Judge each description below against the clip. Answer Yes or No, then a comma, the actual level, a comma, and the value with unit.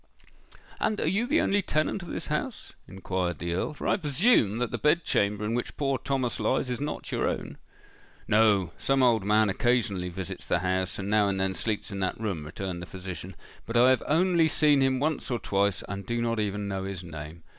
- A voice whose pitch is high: No, low, 110 Hz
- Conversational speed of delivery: No, fast, 215 wpm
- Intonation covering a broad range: Yes, wide, 6.2 semitones